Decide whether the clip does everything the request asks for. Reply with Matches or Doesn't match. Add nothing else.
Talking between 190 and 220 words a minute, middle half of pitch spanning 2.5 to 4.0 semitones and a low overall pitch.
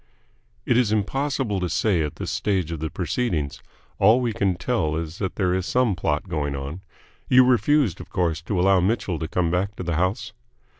Doesn't match